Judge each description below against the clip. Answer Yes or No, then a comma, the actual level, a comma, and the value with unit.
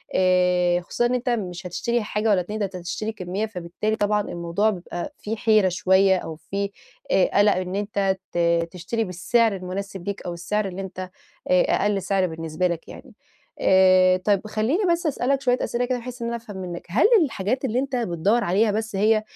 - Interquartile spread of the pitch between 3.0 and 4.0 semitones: Yes, average, 3.3 semitones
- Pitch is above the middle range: Yes, high, 195 Hz